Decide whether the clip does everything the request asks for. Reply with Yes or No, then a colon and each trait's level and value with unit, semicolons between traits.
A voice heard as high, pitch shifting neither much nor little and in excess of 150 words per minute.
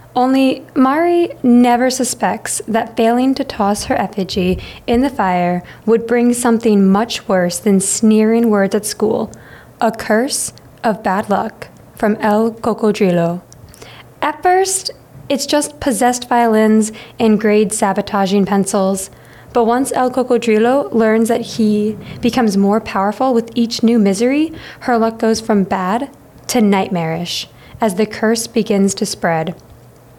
No: high, 225 Hz; average, 3.1 semitones; slow, 135 wpm